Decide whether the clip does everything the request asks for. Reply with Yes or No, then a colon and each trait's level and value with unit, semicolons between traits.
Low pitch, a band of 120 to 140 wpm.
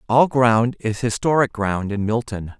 No: low, 115 Hz; average, 160 wpm